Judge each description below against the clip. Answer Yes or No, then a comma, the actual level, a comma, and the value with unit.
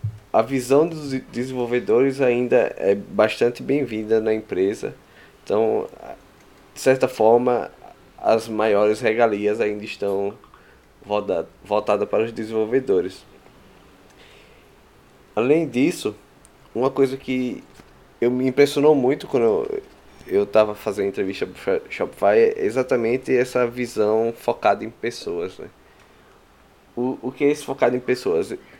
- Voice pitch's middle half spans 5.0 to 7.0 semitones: No, average, 3.9 semitones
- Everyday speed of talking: No, slow, 115 wpm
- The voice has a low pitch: Yes, low, 125 Hz